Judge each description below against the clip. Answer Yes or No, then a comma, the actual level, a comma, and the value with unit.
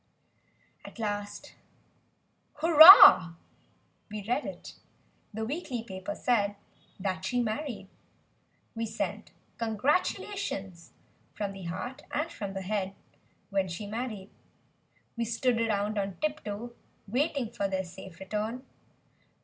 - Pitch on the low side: No, high, 215 Hz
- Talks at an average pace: No, slow, 115 wpm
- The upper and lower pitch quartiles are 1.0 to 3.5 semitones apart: No, average, 4.1 semitones